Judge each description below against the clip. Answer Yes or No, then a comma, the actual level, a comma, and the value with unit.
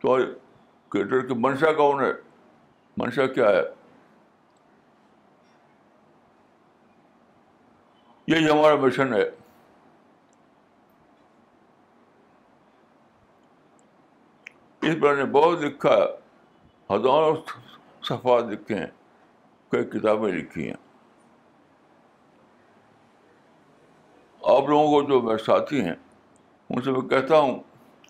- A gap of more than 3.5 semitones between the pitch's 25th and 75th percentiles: No, average, 3.1 semitones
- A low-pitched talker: No, medium, 145 Hz